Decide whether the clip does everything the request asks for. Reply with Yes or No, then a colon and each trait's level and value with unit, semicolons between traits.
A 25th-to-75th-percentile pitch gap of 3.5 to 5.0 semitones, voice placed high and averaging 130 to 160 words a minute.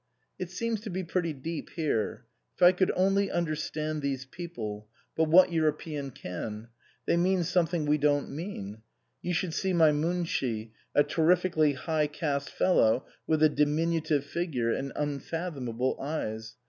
No: average, 4.0 semitones; medium, 155 Hz; average, 155 wpm